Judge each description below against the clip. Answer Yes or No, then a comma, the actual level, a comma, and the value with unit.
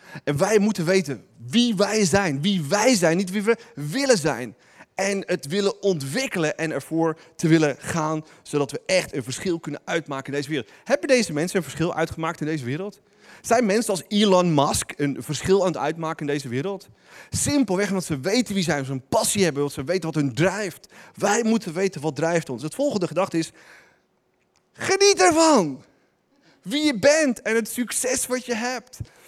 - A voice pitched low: No, medium, 185 Hz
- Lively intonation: Yes, wide, 5.7 semitones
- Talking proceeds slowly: No, average, 195 wpm